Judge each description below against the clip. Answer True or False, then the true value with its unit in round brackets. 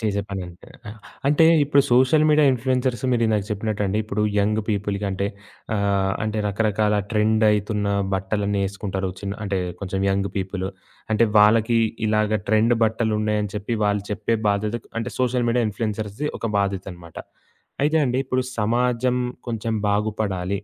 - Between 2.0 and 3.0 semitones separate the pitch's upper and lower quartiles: True (2.4 semitones)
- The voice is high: False (105 Hz)